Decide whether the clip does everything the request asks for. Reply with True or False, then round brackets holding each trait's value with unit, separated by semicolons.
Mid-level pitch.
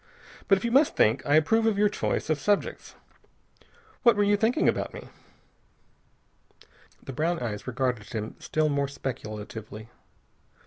True (150 Hz)